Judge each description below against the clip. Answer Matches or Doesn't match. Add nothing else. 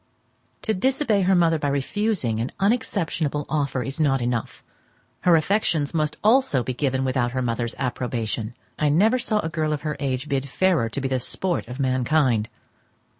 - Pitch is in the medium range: Matches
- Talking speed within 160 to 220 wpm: Matches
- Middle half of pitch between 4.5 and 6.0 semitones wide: Matches